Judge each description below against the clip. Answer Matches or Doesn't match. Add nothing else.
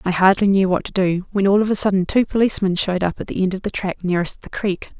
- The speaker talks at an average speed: Doesn't match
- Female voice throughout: Matches